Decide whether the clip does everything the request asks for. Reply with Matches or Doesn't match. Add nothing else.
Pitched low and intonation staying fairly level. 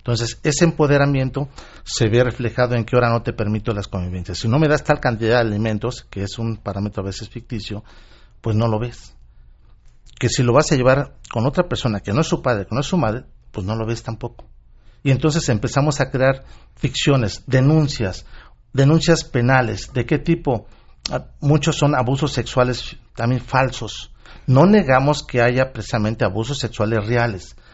Doesn't match